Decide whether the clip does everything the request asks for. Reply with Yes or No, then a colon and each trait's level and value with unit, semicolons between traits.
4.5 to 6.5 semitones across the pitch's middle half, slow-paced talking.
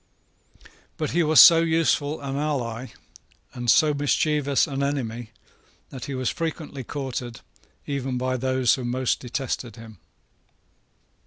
No: average, 3.0 semitones; slow, 130 wpm